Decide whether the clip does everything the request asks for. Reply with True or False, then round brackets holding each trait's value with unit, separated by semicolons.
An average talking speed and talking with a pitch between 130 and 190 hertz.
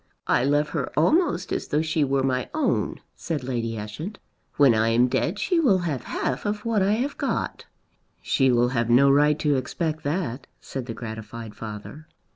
True (185 wpm; 140 Hz)